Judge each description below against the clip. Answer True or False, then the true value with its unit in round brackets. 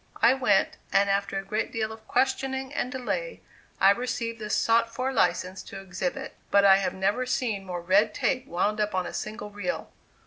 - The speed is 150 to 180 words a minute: False (195 wpm)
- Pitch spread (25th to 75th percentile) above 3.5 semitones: True (4.3 semitones)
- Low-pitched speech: False (215 Hz)